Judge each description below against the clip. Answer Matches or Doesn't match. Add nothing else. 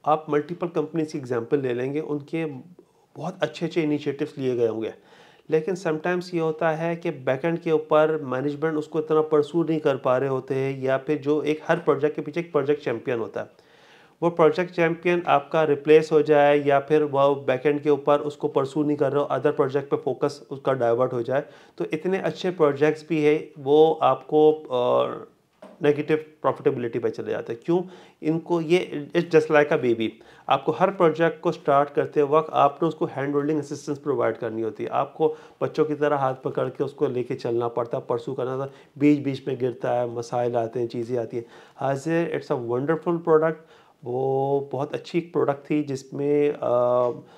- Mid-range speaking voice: Matches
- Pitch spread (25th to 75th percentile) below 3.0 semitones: Matches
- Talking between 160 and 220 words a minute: Matches